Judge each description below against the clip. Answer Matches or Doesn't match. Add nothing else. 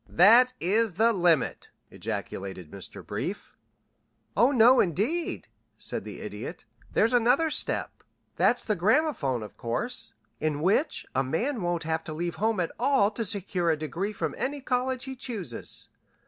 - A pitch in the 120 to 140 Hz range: Doesn't match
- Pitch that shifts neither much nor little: Doesn't match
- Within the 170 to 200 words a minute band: Doesn't match